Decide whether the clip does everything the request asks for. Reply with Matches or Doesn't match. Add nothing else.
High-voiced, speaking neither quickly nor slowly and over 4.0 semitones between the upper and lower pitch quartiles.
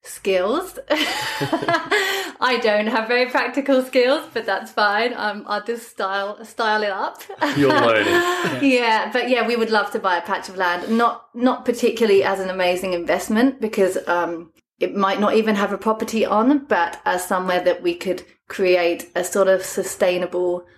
Matches